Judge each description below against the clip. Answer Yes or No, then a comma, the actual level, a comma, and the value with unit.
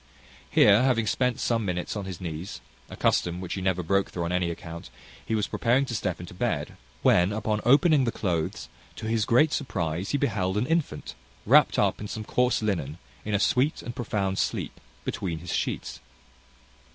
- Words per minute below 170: No, average, 190 wpm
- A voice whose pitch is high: No, low, 100 Hz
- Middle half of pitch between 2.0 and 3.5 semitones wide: No, average, 5.0 semitones